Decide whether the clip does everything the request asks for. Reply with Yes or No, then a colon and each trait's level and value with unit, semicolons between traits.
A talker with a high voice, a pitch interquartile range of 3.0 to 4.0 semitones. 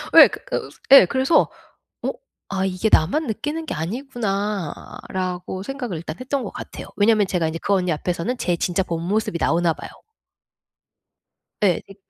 No: high, 195 Hz; wide, 5.4 semitones